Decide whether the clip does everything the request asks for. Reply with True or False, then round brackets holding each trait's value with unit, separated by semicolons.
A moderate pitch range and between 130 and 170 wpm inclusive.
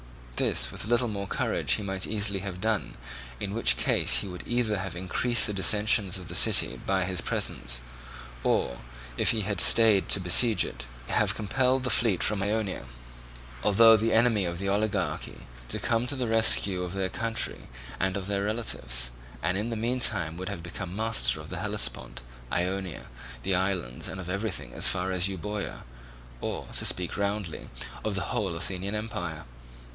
False (3.2 semitones; 180 wpm)